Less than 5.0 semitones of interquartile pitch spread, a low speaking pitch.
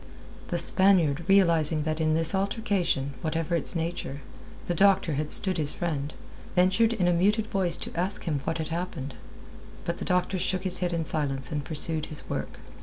No: average, 3.4 semitones; medium, 170 Hz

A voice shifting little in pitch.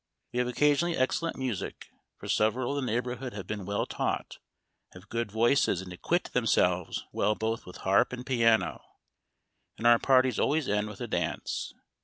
No: average, 3.8 semitones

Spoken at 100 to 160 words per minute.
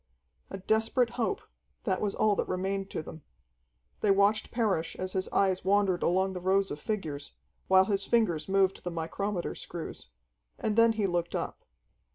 No: average, 170 wpm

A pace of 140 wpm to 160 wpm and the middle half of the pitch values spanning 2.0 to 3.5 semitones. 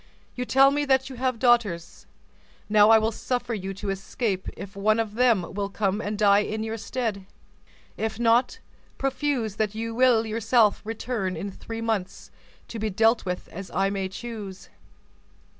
No: average, 170 wpm; average, 3.0 semitones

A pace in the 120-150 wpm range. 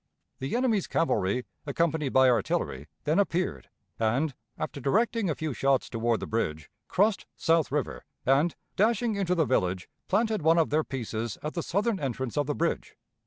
No: average, 165 wpm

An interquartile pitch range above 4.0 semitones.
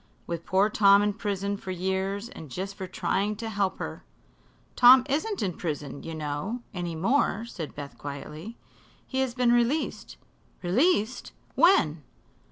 Yes: wide, 5.6 semitones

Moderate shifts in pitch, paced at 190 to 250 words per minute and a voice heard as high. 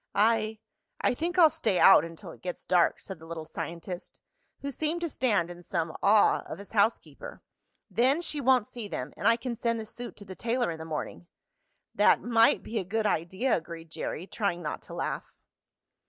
No: wide, 5.9 semitones; average, 200 wpm; high, 210 Hz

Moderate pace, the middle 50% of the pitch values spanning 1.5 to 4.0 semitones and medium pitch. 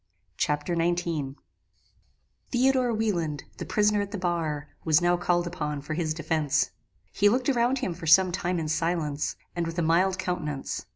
Yes: average, 165 wpm; average, 3.4 semitones; medium, 175 Hz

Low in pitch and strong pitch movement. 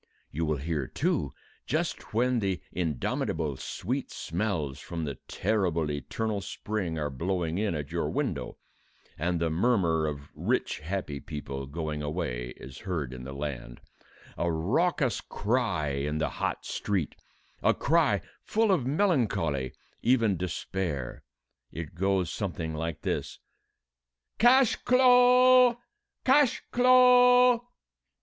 Yes: very low, 85 Hz; wide, 8.3 semitones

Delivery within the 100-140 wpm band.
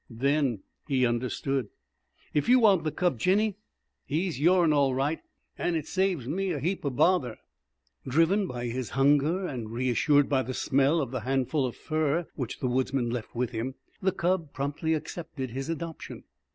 No: average, 175 wpm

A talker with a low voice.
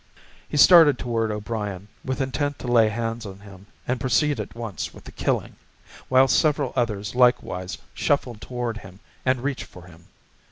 Yes: low, 115 Hz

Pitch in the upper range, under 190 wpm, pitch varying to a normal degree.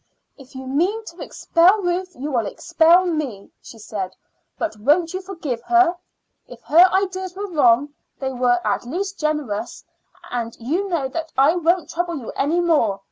No: very high, 320 Hz; average, 170 wpm; wide, 5.9 semitones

